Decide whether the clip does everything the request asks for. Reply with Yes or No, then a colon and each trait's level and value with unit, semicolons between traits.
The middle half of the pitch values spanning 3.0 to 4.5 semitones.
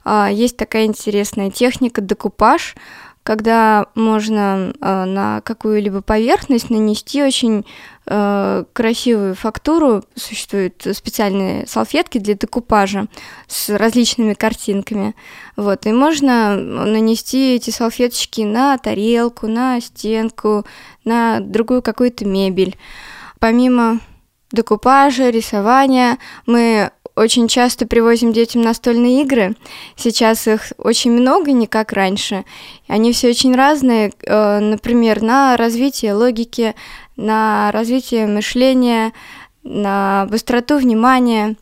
No: narrow, 2.5 semitones